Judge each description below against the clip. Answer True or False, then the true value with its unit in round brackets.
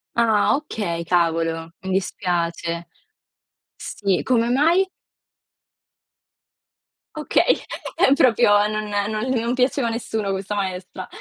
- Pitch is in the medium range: False (205 Hz)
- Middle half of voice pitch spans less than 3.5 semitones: False (4.7 semitones)